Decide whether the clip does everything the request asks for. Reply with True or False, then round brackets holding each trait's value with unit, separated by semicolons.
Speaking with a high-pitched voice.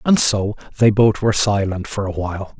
False (105 Hz)